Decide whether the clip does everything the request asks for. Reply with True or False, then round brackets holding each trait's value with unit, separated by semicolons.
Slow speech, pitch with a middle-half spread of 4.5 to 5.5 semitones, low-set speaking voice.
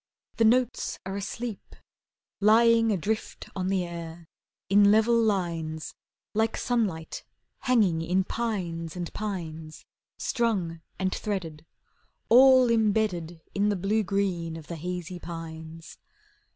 False (115 wpm; 4.8 semitones; 190 Hz)